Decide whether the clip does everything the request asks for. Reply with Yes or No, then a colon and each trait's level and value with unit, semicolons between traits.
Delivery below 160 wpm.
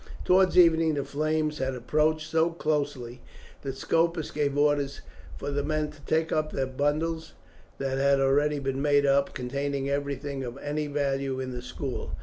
No: average, 165 wpm